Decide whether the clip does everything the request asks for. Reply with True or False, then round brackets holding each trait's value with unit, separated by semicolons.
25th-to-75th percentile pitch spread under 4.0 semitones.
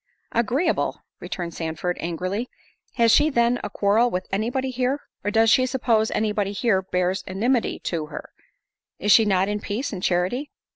False (4.6 semitones)